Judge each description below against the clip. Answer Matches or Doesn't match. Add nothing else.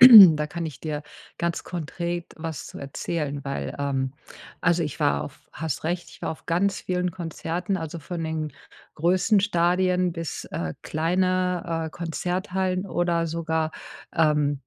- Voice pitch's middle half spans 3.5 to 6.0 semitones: Doesn't match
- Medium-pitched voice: Matches